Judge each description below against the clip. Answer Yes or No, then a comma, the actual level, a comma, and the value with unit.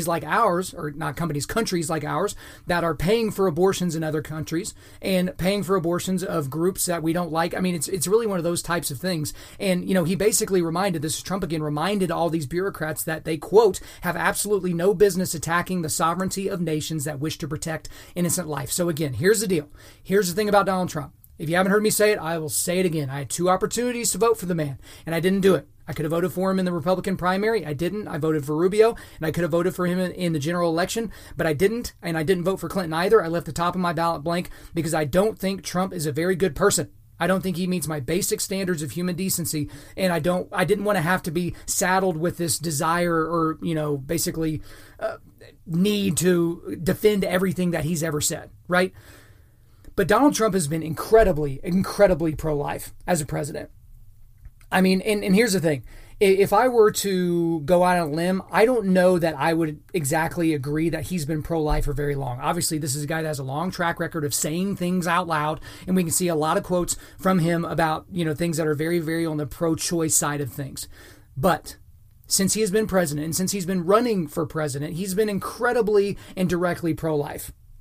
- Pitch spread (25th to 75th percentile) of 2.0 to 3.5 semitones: Yes, average, 3.2 semitones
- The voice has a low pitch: No, medium, 170 Hz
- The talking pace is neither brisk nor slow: No, fast, 230 wpm